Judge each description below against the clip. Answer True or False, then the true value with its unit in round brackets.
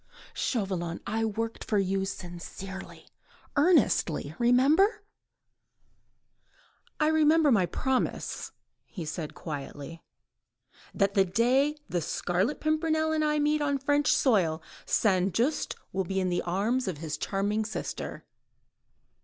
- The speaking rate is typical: False (120 wpm)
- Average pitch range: False (8.4 semitones)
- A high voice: True (215 Hz)